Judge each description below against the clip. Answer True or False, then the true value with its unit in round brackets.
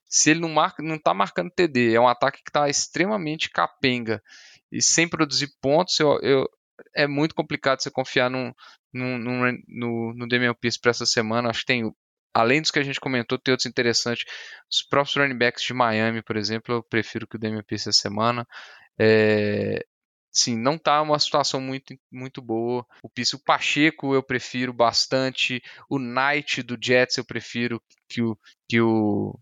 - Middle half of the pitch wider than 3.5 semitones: False (3.1 semitones)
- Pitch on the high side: False (125 Hz)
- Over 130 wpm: True (175 wpm)